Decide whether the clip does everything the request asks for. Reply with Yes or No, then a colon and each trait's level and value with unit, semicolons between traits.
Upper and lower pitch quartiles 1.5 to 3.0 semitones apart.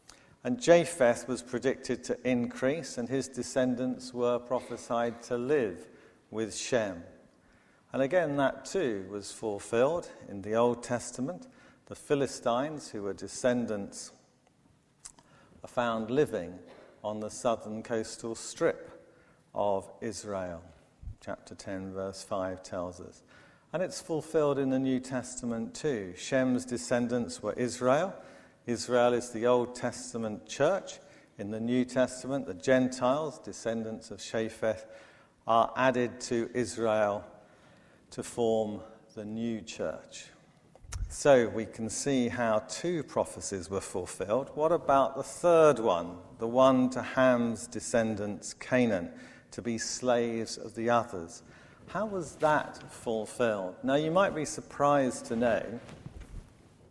Yes: narrow, 2.6 semitones